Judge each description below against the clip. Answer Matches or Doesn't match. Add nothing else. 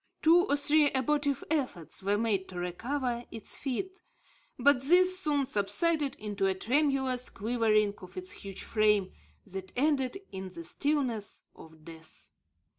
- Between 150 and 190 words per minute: Doesn't match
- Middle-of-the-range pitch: Doesn't match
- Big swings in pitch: Matches